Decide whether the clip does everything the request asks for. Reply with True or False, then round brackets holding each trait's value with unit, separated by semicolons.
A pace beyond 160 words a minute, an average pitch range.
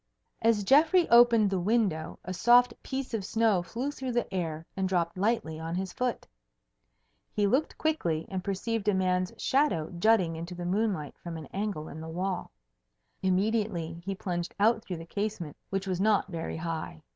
True (175 wpm; 4.8 semitones)